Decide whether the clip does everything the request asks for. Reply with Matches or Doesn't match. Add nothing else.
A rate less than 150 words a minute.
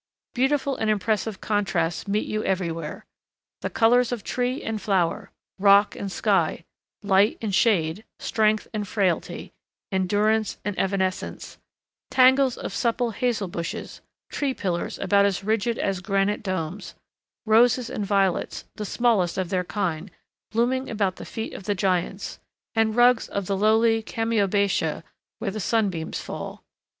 Matches